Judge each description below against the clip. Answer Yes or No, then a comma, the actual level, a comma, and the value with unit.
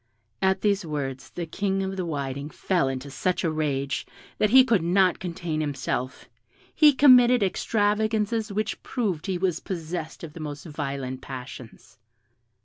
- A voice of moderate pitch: Yes, medium, 175 Hz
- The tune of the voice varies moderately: No, wide, 6.1 semitones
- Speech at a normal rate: Yes, average, 150 wpm